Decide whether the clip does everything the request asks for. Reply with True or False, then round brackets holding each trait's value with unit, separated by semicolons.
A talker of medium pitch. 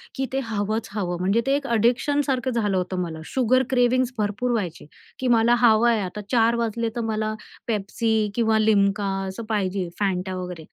False (220 Hz)